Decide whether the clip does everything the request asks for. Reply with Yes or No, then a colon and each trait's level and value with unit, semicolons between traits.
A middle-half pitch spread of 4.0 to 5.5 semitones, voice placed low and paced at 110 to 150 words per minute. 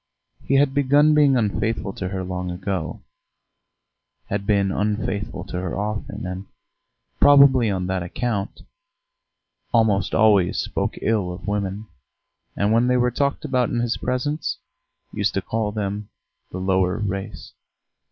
Yes: average, 4.3 semitones; low, 105 Hz; average, 140 wpm